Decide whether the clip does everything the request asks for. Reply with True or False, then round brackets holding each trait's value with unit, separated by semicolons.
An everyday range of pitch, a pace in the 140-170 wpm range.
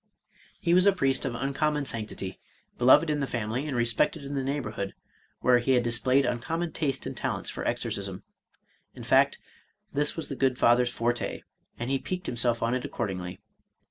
False (3.5 semitones; 180 wpm)